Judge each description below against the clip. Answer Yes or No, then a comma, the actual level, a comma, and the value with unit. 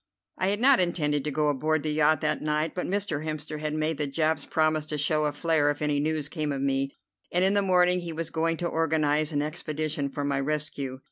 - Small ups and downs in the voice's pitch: Yes, narrow, 1.8 semitones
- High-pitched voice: No, medium, 155 Hz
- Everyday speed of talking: No, fast, 230 wpm